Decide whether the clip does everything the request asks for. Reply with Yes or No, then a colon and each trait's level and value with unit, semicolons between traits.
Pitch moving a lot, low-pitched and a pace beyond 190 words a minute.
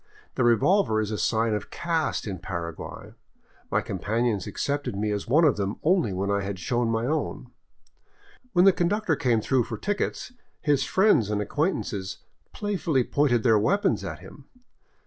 No: wide, 7.6 semitones; low, 120 Hz; average, 170 wpm